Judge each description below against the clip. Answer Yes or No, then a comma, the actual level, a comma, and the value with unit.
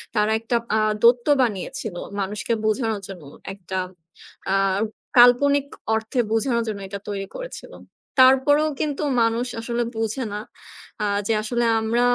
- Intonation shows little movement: No, average, 3.3 semitones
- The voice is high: Yes, high, 230 Hz